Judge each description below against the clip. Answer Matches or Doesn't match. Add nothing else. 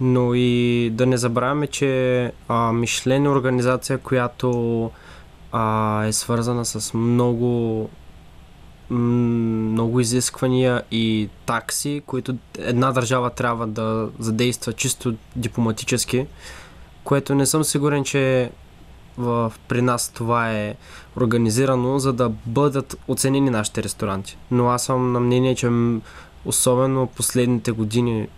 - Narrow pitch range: Matches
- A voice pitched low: Matches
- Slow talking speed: Matches